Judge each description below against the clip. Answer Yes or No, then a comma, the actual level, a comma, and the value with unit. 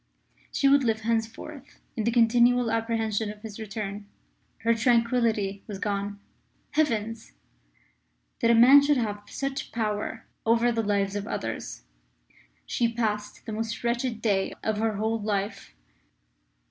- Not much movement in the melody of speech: Yes, narrow, 2.2 semitones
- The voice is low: No, high, 225 Hz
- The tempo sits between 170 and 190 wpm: No, slow, 135 wpm